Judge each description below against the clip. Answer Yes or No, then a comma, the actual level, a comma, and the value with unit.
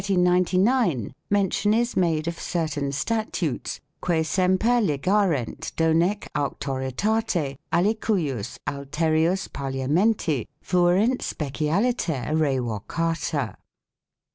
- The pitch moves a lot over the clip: Yes, wide, 5.8 semitones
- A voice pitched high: No, medium, 165 Hz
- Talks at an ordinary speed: No, slow, 85 wpm